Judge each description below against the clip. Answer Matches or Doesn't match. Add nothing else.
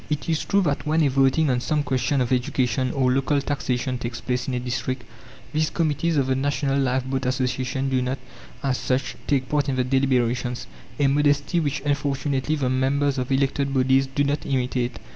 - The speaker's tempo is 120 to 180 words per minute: Doesn't match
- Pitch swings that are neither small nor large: Doesn't match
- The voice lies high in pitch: Doesn't match